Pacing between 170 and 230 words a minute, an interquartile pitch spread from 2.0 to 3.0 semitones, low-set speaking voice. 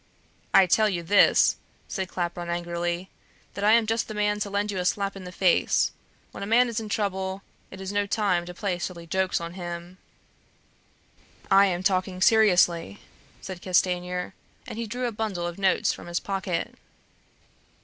No: average, 180 wpm; average, 2.7 semitones; high, 190 Hz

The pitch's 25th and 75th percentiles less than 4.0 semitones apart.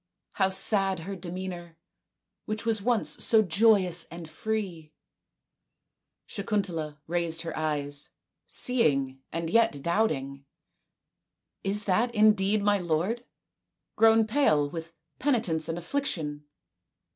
No: average, 5.2 semitones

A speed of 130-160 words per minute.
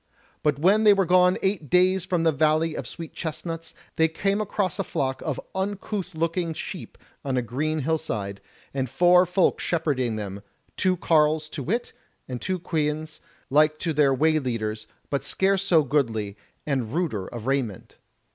No: average, 170 wpm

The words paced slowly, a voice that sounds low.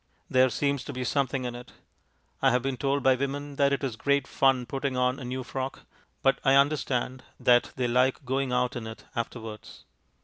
No: average, 200 wpm; low, 130 Hz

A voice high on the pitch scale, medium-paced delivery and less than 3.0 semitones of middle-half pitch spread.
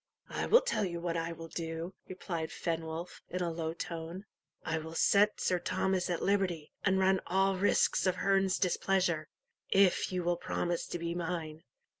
No: medium, 175 Hz; average, 175 wpm; narrow, 2.4 semitones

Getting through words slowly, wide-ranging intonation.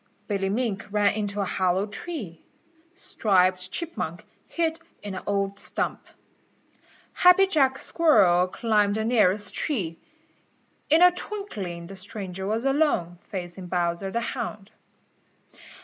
Yes: slow, 120 wpm; wide, 6.3 semitones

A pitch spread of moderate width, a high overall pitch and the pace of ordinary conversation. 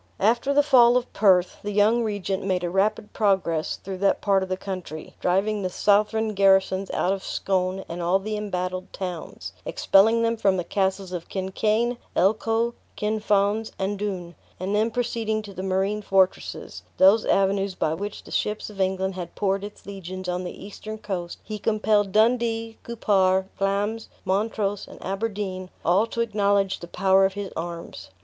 No: narrow, 2.3 semitones; high, 195 Hz; average, 170 wpm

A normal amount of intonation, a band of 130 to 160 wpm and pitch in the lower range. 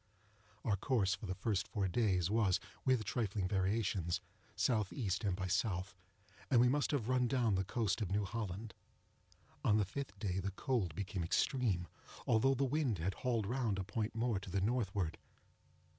No: average, 4.0 semitones; average, 175 wpm; low, 105 Hz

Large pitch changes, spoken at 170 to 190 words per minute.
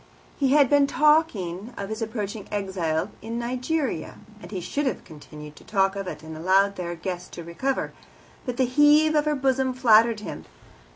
Yes: wide, 6.4 semitones; average, 180 wpm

